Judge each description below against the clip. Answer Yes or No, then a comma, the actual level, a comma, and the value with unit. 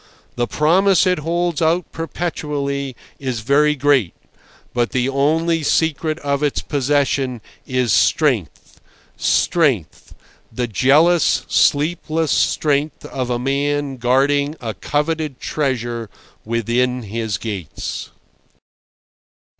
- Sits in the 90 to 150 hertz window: Yes, medium, 140 Hz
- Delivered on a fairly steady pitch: No, average, 3.9 semitones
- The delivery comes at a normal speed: No, slow, 100 wpm